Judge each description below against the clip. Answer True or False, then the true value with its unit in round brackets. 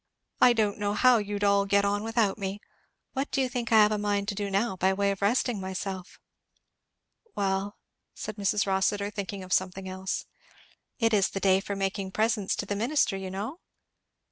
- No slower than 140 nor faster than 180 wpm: False (195 wpm)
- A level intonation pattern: True (1.9 semitones)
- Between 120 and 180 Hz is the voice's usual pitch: False (200 Hz)